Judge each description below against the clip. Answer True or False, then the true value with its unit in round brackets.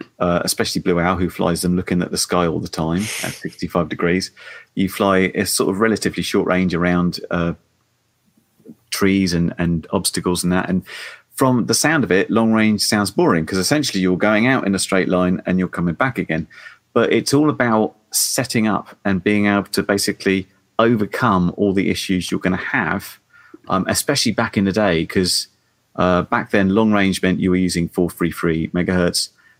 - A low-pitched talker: True (95 Hz)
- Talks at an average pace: True (190 wpm)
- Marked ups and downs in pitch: False (2.6 semitones)